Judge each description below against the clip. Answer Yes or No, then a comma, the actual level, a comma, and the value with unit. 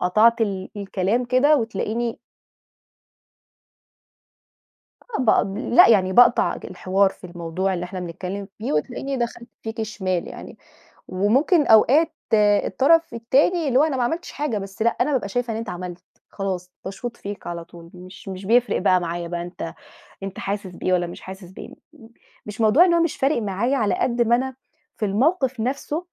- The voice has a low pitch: No, high, 215 Hz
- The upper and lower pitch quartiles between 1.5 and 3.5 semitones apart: No, average, 5.1 semitones